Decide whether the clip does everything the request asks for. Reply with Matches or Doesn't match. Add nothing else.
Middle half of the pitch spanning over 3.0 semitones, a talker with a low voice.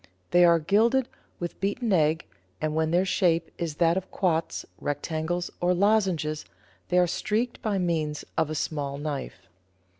Doesn't match